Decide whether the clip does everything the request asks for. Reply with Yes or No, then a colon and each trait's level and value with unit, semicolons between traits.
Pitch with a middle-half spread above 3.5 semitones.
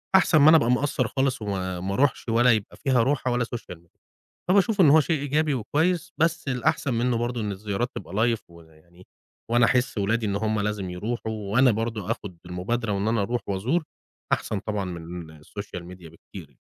Yes: average, 5.2 semitones